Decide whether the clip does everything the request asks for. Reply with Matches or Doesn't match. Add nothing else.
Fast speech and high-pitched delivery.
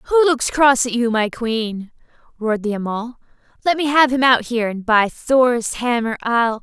Doesn't match